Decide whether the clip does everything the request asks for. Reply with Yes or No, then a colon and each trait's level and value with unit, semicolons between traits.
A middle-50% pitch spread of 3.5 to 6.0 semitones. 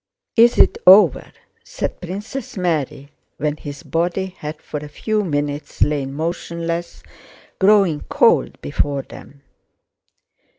Yes: average, 4.5 semitones